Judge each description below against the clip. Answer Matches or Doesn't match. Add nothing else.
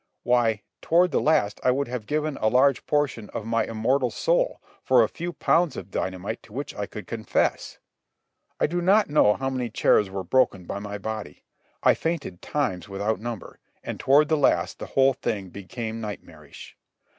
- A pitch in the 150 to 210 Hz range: Doesn't match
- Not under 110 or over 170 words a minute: Doesn't match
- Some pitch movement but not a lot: Doesn't match